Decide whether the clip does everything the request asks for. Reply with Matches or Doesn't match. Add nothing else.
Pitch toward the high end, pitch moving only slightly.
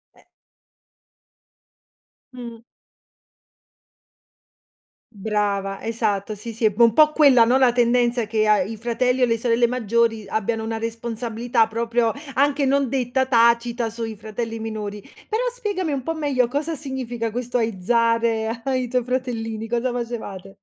Matches